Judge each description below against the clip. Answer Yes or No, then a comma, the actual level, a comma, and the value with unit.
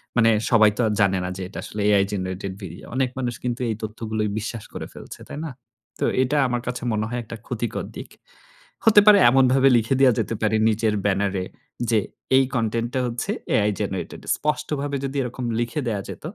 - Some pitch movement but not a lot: Yes, average, 3.3 semitones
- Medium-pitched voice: No, low, 115 Hz